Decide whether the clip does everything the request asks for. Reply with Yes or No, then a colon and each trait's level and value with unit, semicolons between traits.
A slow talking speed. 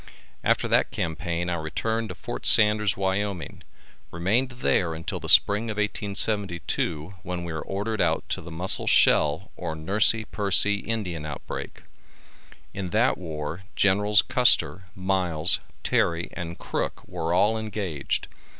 Yes: slow, 130 wpm